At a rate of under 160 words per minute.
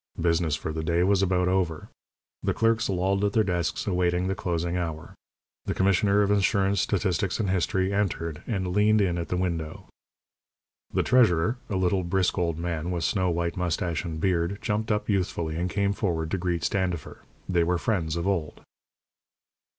No: average, 175 wpm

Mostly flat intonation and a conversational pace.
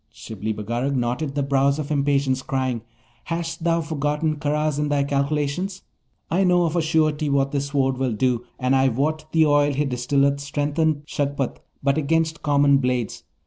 Yes: narrow, 2.3 semitones; average, 170 wpm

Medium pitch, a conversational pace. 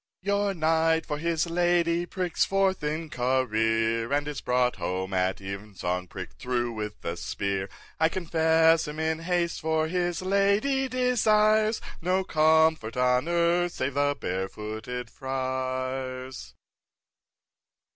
No: medium, 155 Hz; slow, 125 wpm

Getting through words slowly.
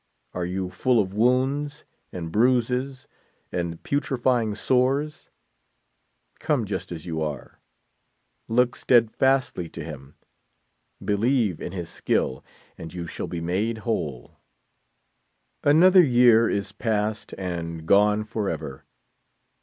Yes: slow, 115 wpm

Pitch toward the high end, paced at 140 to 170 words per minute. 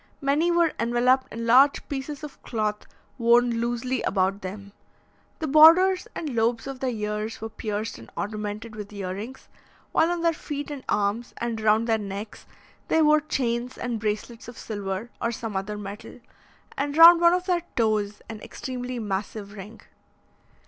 Yes: high, 230 Hz; average, 165 wpm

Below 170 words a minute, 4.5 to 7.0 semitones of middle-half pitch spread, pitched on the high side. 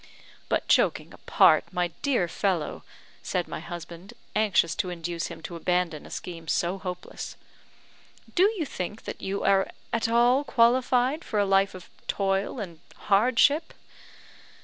Yes: average, 145 wpm; average, 5.2 semitones; high, 195 Hz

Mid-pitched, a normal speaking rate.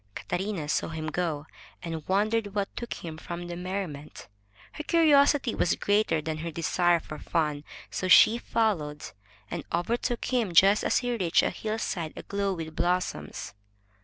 Yes: medium, 180 Hz; average, 155 wpm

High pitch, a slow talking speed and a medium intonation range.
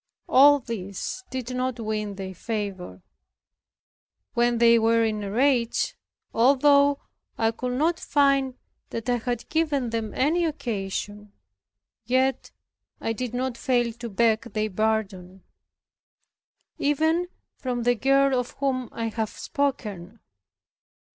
Yes: high, 235 Hz; slow, 120 wpm; average, 3.6 semitones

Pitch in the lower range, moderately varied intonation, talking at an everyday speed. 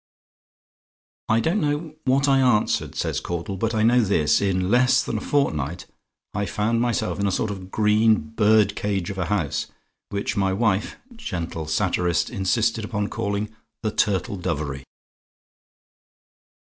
Yes: low, 105 Hz; average, 3.4 semitones; average, 150 wpm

